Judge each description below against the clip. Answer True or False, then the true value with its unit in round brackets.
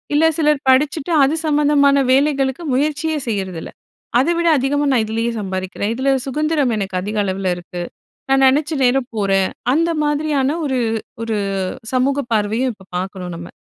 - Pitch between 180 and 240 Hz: False (265 Hz)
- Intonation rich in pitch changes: True (6.2 semitones)